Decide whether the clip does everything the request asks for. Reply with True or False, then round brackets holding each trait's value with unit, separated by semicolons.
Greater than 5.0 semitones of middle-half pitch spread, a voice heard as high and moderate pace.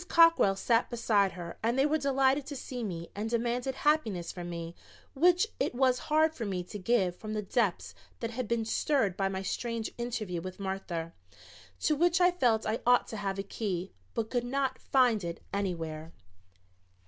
True (5.5 semitones; 225 Hz; 185 wpm)